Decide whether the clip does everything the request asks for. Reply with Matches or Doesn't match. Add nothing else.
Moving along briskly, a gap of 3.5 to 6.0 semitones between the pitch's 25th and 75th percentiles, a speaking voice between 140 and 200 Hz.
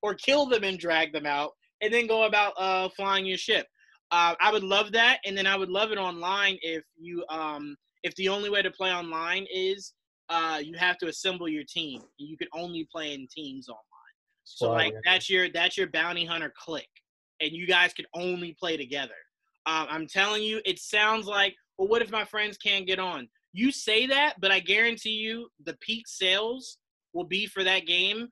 Matches